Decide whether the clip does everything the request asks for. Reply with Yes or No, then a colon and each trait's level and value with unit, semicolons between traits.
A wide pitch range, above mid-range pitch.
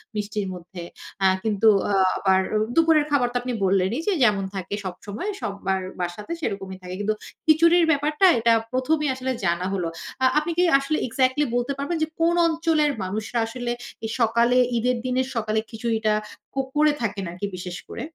Yes: wide, 6.8 semitones; high, 230 Hz